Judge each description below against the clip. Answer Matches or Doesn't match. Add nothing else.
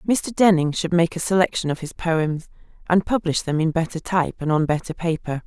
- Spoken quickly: Matches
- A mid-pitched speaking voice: Matches